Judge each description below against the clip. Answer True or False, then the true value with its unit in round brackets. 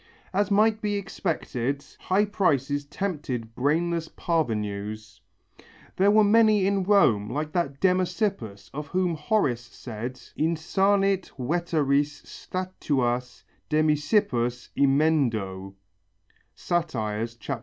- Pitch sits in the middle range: True (150 Hz)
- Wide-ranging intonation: True (7.4 semitones)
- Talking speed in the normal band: False (90 wpm)